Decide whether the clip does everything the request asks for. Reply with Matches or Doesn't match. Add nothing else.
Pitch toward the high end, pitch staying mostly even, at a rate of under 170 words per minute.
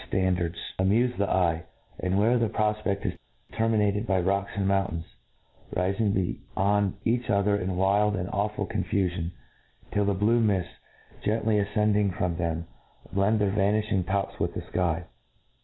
Doesn't match